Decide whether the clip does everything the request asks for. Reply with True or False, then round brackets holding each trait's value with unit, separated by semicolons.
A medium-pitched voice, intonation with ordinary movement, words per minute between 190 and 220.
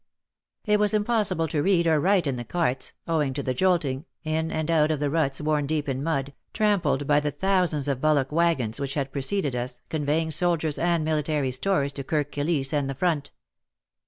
True (150 Hz; 3.4 semitones; 200 wpm)